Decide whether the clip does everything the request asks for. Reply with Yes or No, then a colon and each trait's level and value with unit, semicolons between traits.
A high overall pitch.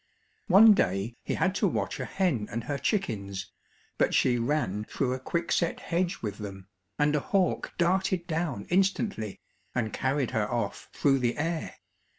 No: medium, 140 Hz